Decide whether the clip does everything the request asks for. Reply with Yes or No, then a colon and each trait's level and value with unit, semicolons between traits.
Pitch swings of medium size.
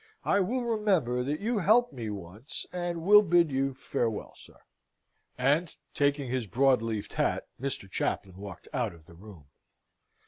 No: wide, 8.2 semitones